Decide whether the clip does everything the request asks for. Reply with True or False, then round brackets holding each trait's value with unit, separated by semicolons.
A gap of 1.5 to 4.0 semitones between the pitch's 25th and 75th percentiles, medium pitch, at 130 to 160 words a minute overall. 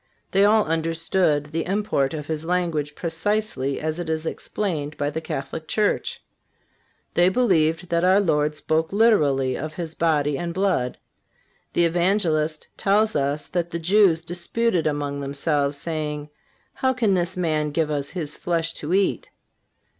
True (3.5 semitones; 165 Hz; 150 wpm)